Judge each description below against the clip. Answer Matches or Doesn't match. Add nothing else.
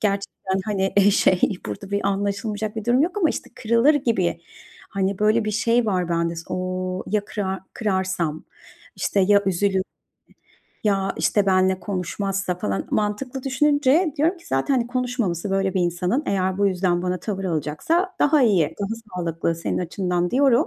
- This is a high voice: Matches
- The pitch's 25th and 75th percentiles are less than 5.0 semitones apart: Matches